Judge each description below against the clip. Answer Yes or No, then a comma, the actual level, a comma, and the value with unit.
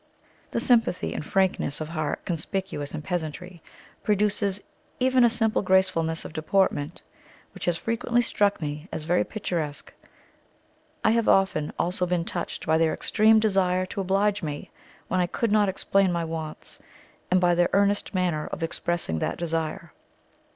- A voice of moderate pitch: Yes, medium, 180 Hz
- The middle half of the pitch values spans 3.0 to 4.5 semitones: Yes, average, 3.7 semitones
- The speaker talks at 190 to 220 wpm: No, average, 160 wpm